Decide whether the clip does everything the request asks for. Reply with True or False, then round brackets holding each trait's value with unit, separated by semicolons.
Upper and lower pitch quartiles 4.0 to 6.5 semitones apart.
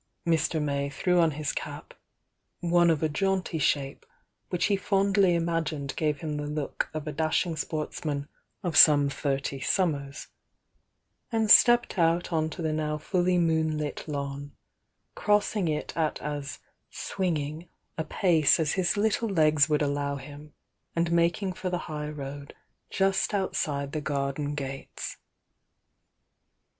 False (3.3 semitones)